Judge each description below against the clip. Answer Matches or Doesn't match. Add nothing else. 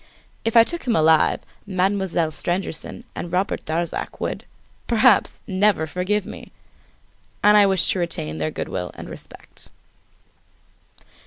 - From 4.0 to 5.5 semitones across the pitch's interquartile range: Matches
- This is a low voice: Doesn't match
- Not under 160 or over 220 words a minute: Doesn't match